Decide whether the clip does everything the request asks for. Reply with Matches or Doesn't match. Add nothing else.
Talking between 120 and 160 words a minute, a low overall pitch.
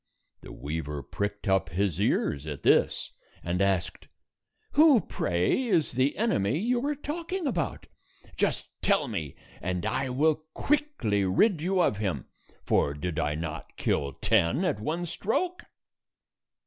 Matches